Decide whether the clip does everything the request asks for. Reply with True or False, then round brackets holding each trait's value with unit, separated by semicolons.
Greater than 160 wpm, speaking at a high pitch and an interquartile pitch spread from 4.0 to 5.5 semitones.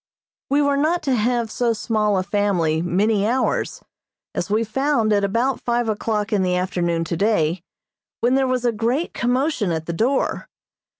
True (170 wpm; 220 Hz; 4.4 semitones)